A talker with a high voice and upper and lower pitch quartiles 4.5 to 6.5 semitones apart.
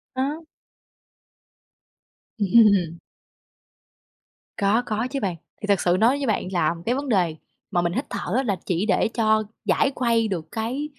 Yes: high, 215 Hz; average, 4.9 semitones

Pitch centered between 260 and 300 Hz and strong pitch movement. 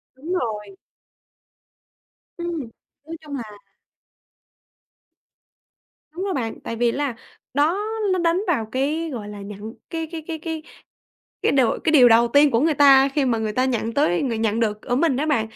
Yes: very high, 270 Hz; wide, 5.7 semitones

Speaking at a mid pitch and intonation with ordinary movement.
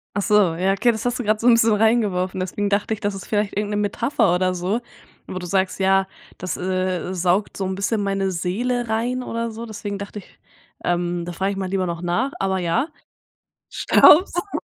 No: high, 200 Hz; average, 3.1 semitones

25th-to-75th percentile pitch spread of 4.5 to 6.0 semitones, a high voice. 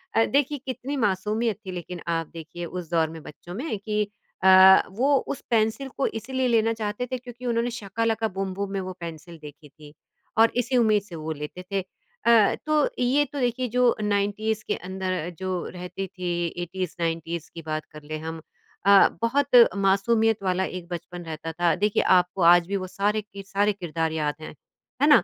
Yes: average, 4.8 semitones; high, 195 Hz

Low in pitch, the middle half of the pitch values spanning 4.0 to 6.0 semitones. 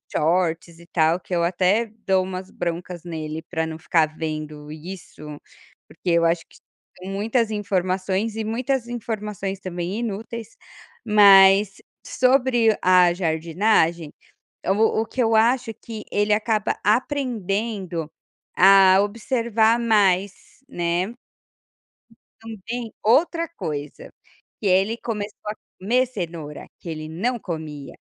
No: high, 195 Hz; average, 4.7 semitones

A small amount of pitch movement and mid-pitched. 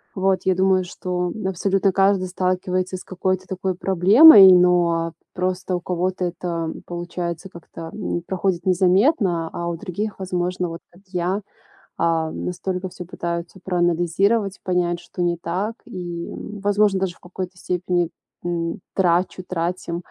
Yes: narrow, 1.6 semitones; medium, 180 Hz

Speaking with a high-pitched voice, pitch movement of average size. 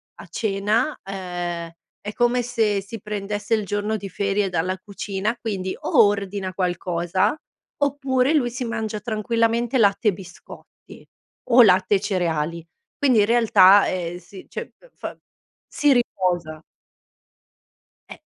Yes: high, 205 Hz; average, 3.7 semitones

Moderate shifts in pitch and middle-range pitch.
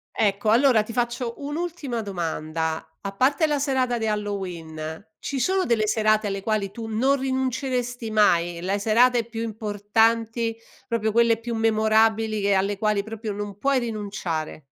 No: average, 3.1 semitones; high, 220 Hz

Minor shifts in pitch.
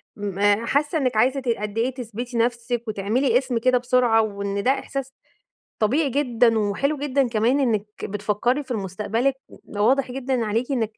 No: average, 3.5 semitones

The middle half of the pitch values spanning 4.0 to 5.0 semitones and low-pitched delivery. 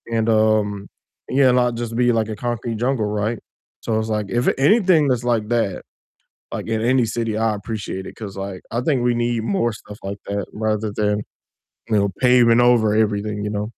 No: narrow, 2.5 semitones; low, 110 Hz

